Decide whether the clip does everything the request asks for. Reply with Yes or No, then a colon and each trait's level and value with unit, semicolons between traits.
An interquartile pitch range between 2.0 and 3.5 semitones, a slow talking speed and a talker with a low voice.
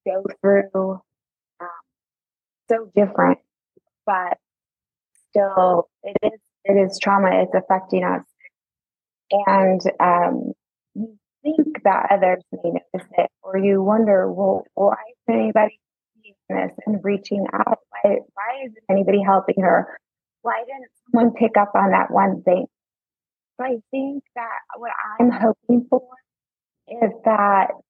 No: average, 3.1 semitones; slow, 130 wpm; high, 205 Hz